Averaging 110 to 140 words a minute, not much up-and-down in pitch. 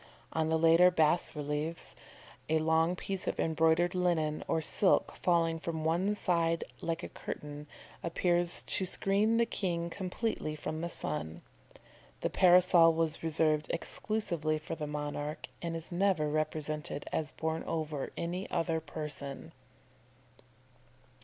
Yes: slow, 135 wpm; narrow, 2.2 semitones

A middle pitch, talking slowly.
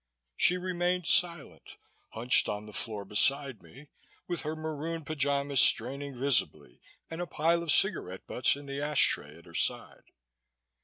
No: medium, 145 Hz; average, 155 wpm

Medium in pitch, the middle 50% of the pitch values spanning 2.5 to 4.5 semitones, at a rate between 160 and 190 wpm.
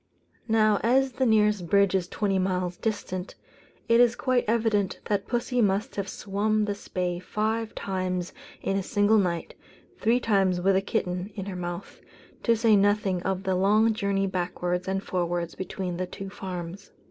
No: high, 195 Hz; average, 2.9 semitones; average, 170 wpm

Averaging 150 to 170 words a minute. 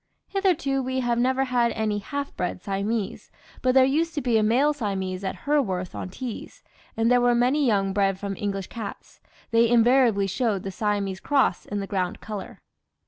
No: average, 185 wpm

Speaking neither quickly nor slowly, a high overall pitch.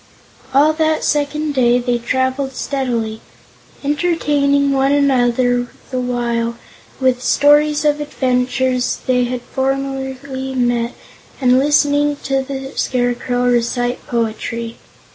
No: slow, 105 wpm; very high, 260 Hz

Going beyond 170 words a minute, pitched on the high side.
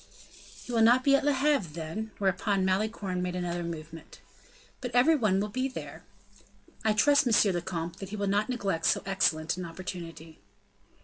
Yes: average, 180 wpm; high, 195 Hz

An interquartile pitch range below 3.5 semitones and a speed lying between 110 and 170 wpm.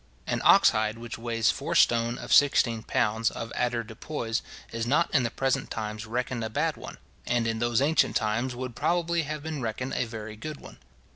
No: average, 2.7 semitones; average, 195 wpm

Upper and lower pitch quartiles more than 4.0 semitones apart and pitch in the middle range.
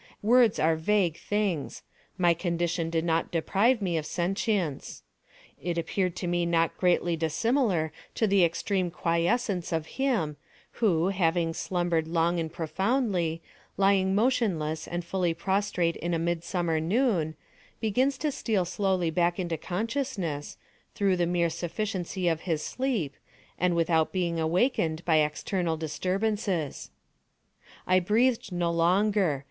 No: average, 3.3 semitones; medium, 175 Hz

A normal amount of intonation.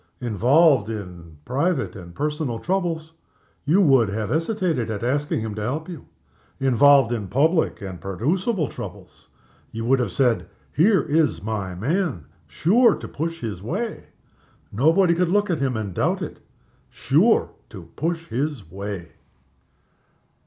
No: wide, 7.4 semitones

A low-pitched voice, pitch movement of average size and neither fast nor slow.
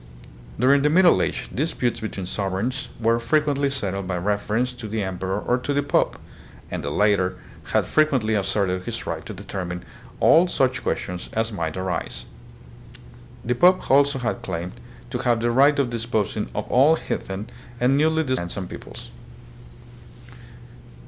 No: low, 115 Hz; wide, 6.1 semitones; average, 160 wpm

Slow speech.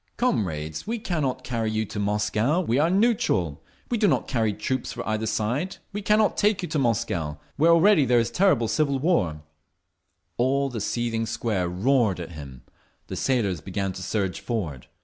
No: average, 175 wpm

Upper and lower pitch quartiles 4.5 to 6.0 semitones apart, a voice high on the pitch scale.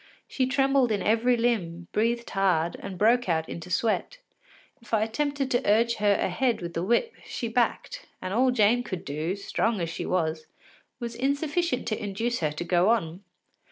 Yes: average, 5.1 semitones; high, 220 Hz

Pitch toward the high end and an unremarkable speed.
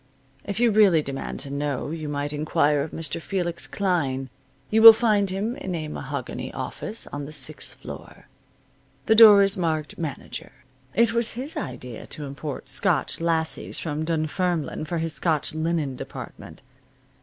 No: medium, 160 Hz; average, 155 wpm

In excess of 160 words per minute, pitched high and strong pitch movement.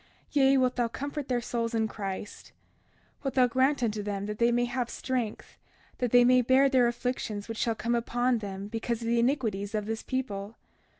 No: average, 200 wpm; high, 235 Hz; average, 2.7 semitones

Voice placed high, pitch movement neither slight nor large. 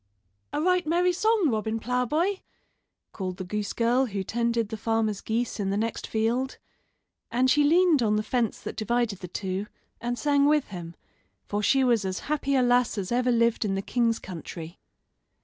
Yes: high, 235 Hz; average, 4.2 semitones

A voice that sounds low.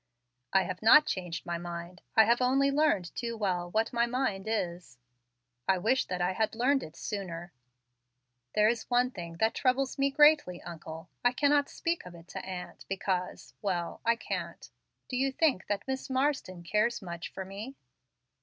No: high, 210 Hz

